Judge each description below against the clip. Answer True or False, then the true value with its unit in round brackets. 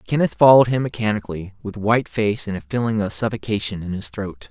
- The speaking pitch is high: False (110 Hz)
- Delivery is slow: False (200 wpm)